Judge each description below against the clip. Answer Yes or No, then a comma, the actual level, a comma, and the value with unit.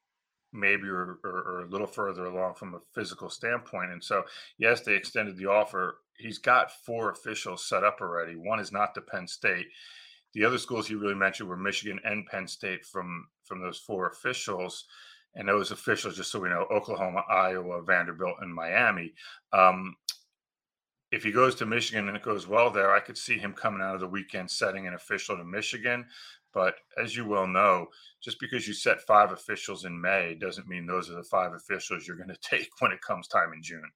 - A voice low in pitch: Yes, very low, 95 Hz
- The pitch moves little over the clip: No, average, 3.0 semitones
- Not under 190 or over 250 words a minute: Yes, fast, 205 wpm